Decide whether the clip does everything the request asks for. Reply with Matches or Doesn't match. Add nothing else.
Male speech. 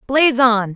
Doesn't match